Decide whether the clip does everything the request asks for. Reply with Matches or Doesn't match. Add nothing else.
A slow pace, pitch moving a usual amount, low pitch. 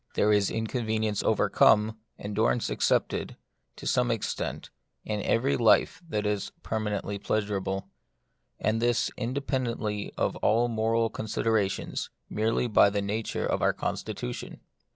Doesn't match